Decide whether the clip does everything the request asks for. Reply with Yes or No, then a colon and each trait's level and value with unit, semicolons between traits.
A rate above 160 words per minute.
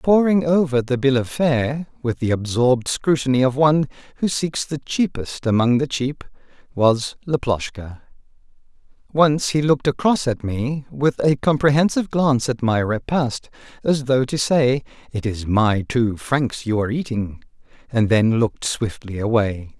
No: average, 155 wpm